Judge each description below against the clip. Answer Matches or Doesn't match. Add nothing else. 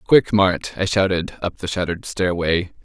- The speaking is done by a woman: Doesn't match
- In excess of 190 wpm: Doesn't match